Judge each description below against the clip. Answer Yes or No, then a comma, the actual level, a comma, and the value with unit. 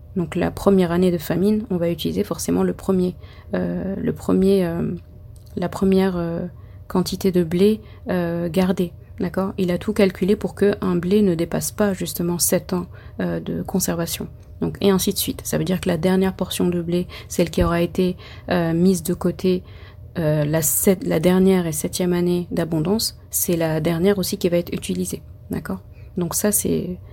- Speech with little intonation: Yes, narrow, 2.1 semitones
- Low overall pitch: No, medium, 180 Hz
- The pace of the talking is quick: No, average, 190 wpm